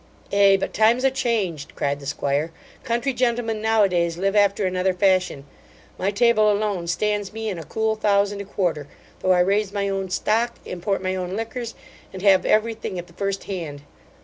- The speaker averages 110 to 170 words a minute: No, average, 195 wpm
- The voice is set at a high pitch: Yes, high, 200 Hz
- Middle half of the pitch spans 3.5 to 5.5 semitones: No, average, 3.0 semitones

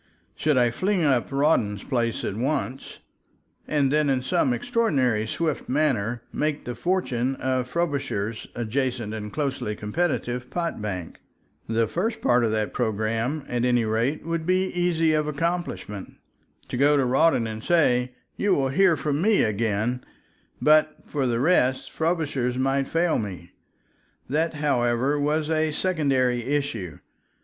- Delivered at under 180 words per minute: Yes, average, 145 wpm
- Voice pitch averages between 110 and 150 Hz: Yes, low, 135 Hz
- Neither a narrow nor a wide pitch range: Yes, average, 4.8 semitones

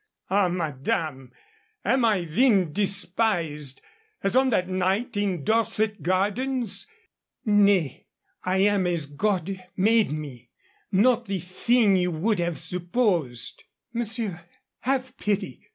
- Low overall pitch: No, high, 195 Hz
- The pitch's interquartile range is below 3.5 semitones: No, average, 4.3 semitones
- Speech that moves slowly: Yes, slow, 120 wpm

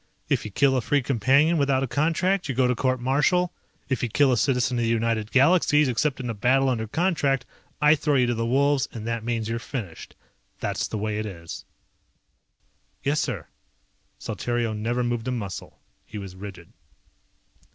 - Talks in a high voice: No, low, 125 Hz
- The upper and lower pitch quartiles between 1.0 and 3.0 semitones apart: No, average, 3.8 semitones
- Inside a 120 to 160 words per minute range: No, average, 185 wpm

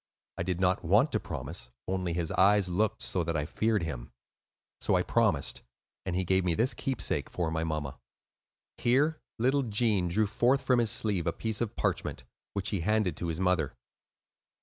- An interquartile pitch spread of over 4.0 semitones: Yes, average, 4.4 semitones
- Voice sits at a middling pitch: No, very low, 95 Hz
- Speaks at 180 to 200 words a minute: Yes, average, 185 wpm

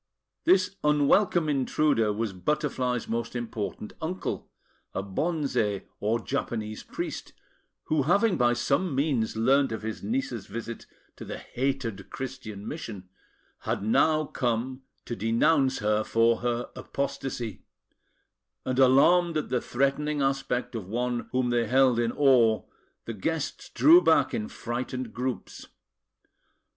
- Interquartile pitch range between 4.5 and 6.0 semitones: No, average, 4.1 semitones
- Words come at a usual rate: No, slow, 130 wpm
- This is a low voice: Yes, low, 125 Hz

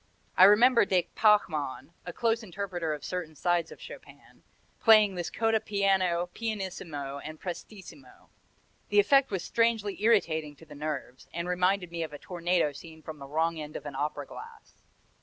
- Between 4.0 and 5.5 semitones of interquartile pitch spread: Yes, average, 4.8 semitones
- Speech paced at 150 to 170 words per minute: Yes, average, 165 wpm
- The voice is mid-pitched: Yes, medium, 175 Hz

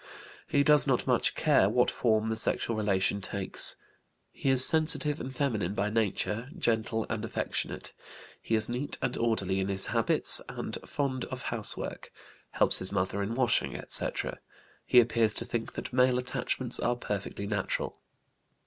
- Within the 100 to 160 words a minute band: Yes, average, 155 wpm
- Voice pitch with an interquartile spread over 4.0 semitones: No, average, 3.6 semitones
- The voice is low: Yes, low, 115 Hz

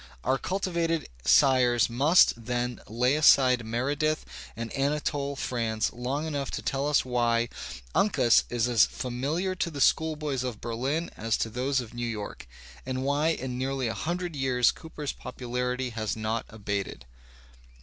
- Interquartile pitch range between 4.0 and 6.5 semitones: No, average, 3.5 semitones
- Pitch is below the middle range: Yes, low, 130 Hz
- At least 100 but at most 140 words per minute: No, average, 155 wpm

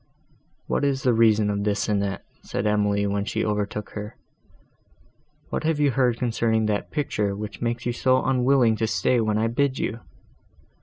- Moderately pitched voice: No, low, 110 Hz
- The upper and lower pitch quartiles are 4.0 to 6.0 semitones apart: No, average, 3.2 semitones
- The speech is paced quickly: No, average, 170 wpm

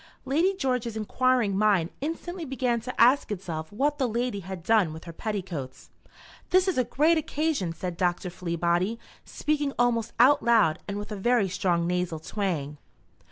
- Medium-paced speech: Yes, average, 160 wpm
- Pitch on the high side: Yes, high, 215 Hz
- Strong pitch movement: Yes, wide, 6.4 semitones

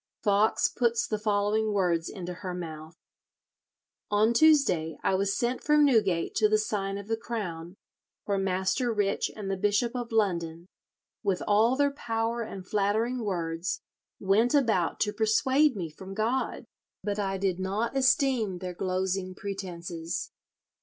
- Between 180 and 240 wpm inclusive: No, average, 145 wpm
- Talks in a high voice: Yes, high, 205 Hz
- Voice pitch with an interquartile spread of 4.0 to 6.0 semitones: No, average, 3.6 semitones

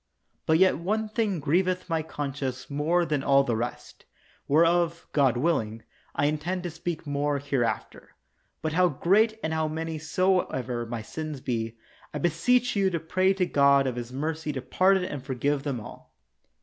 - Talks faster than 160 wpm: Yes, average, 170 wpm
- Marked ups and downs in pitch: No, average, 4.3 semitones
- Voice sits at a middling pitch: Yes, medium, 155 Hz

